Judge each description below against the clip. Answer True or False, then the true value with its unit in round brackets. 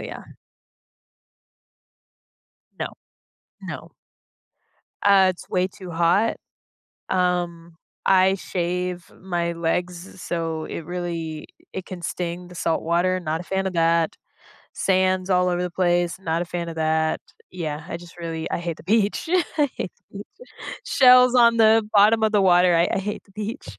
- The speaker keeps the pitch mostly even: True (2.1 semitones)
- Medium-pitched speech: True (180 Hz)